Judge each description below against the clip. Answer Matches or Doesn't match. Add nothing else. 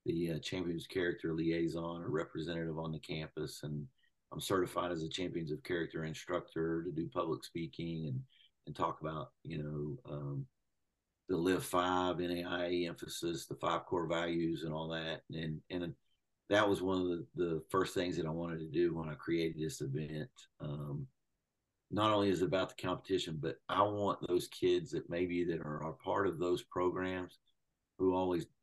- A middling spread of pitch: Doesn't match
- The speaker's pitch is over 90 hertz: Doesn't match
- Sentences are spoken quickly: Doesn't match